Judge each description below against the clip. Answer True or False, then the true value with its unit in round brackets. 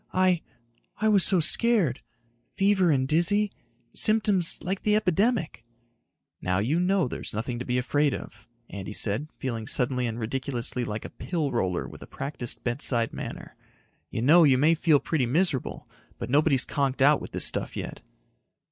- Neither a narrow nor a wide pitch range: False (6.7 semitones)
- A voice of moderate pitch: True (145 Hz)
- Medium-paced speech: True (165 wpm)